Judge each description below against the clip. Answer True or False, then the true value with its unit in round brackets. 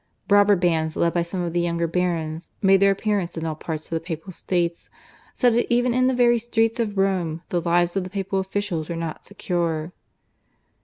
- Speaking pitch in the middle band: True (180 Hz)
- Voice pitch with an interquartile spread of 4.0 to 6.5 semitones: False (3.3 semitones)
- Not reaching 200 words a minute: False (205 wpm)